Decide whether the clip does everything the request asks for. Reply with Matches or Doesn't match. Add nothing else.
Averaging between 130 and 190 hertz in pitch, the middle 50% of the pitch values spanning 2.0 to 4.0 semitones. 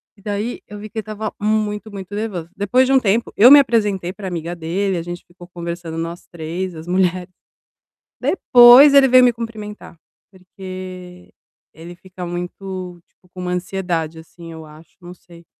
Matches